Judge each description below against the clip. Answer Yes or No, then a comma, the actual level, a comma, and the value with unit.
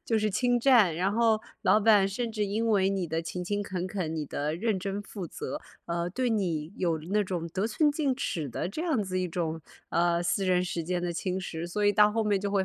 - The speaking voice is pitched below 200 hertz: Yes, high, 190 Hz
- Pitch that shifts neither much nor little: Yes, average, 3.6 semitones